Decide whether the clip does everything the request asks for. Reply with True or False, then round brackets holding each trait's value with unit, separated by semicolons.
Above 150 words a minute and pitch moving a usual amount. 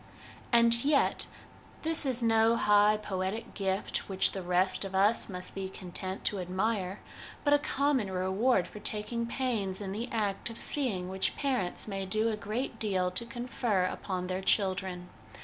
True (165 wpm; 3.7 semitones)